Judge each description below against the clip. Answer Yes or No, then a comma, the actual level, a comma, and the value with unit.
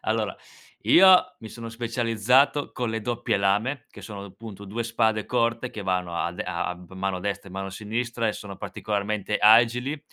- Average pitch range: Yes, average, 3.0 semitones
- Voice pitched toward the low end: Yes, low, 110 Hz